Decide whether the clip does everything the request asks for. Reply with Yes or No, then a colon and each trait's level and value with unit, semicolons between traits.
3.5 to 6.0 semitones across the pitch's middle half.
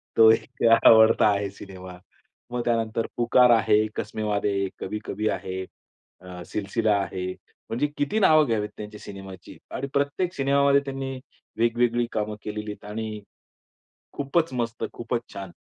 No: average, 3.1 semitones